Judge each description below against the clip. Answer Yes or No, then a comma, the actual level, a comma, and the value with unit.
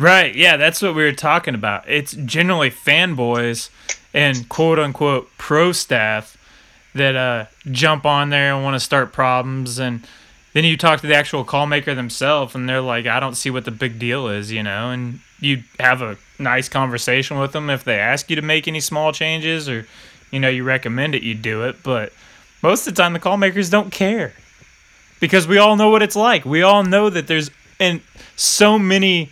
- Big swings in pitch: No, average, 4.3 semitones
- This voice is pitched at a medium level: Yes, medium, 145 Hz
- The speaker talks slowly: No, average, 200 wpm